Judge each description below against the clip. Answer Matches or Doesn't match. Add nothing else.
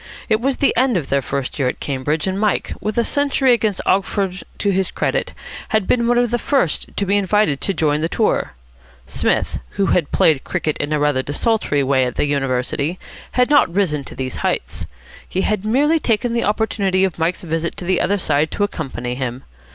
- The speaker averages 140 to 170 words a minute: Doesn't match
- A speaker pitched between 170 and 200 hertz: Matches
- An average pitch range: Doesn't match